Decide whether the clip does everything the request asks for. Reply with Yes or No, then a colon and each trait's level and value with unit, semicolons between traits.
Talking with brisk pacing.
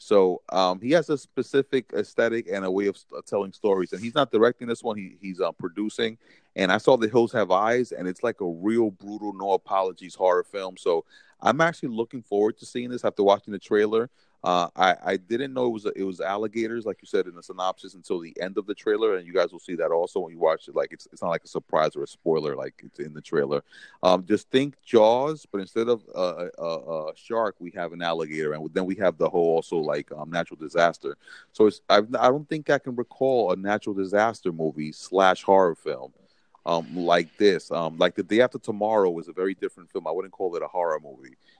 Yes: fast, 240 wpm